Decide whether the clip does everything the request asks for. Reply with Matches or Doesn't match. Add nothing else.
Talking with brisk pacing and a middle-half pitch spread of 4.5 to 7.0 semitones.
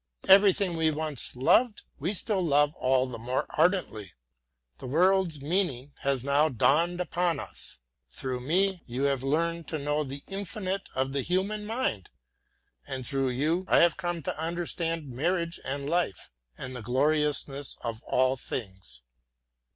Doesn't match